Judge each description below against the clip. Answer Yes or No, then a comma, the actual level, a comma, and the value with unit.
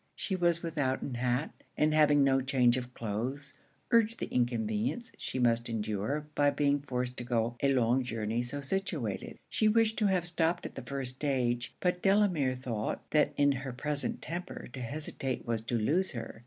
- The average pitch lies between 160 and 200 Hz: No, low, 135 Hz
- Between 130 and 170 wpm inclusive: No, average, 180 wpm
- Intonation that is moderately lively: Yes, average, 4.4 semitones